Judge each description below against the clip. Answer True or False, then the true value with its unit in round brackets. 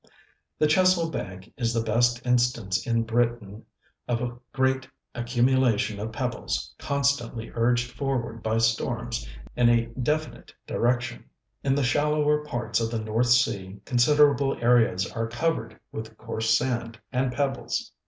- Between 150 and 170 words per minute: False (135 wpm)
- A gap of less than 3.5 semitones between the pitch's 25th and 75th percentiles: True (2.7 semitones)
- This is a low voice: True (120 Hz)